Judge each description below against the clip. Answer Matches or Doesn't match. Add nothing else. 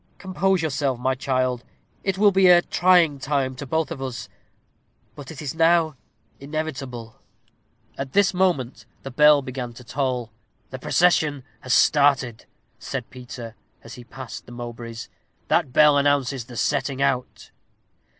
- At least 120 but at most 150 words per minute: Matches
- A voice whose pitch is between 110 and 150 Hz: Matches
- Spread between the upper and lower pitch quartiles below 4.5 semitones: Matches